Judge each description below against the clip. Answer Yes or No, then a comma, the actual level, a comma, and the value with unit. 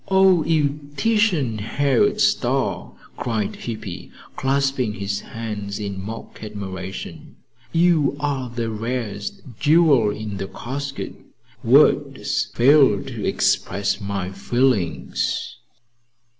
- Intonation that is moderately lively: No, wide, 5.7 semitones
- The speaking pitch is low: Yes, low, 120 Hz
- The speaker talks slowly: Yes, slow, 100 wpm